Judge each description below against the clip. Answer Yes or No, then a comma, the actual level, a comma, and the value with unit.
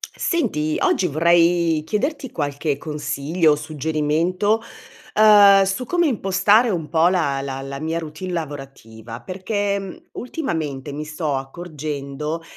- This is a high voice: No, medium, 160 Hz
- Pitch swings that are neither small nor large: Yes, average, 4.7 semitones